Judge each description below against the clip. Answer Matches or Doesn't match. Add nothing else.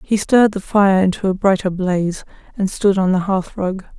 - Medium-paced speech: Matches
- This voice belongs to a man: Doesn't match